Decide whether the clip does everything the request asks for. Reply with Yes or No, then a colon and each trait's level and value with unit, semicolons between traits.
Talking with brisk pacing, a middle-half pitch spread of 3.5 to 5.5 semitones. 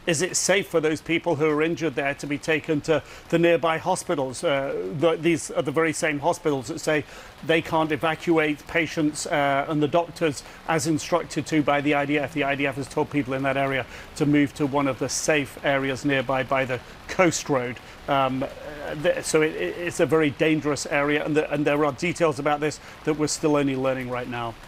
No: fast, 210 wpm; average, 2.7 semitones